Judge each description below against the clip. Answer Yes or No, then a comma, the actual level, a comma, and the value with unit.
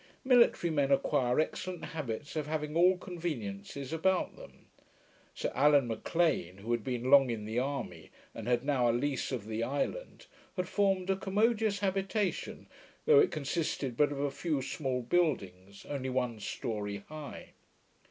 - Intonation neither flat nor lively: No, wide, 6.4 semitones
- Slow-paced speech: No, average, 155 wpm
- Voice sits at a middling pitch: Yes, medium, 145 Hz